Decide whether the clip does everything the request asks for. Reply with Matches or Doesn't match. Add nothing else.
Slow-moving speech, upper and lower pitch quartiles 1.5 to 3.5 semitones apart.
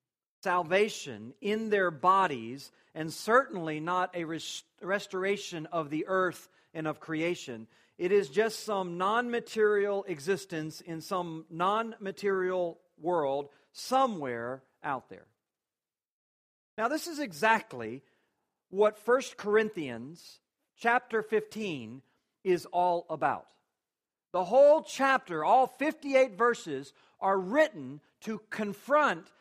Doesn't match